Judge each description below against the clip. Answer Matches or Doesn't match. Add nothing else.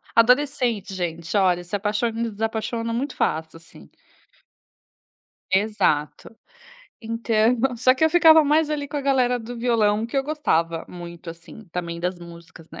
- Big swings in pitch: Matches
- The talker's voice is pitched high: Matches